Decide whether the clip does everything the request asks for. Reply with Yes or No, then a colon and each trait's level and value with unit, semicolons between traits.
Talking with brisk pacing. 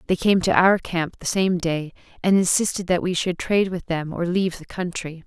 Yes: fast, 230 wpm